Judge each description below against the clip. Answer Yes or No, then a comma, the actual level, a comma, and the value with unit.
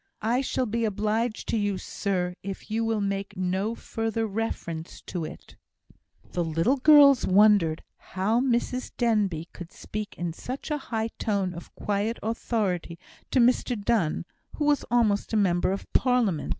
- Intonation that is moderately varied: Yes, average, 3.8 semitones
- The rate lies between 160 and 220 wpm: No, average, 150 wpm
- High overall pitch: Yes, high, 210 Hz